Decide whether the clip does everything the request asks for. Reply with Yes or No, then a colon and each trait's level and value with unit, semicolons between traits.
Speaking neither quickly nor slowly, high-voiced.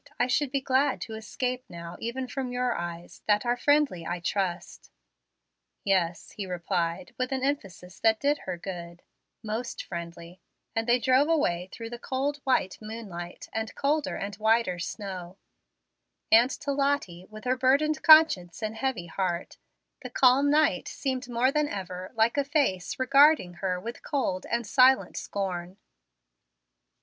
Yes: average, 155 wpm; high, 225 Hz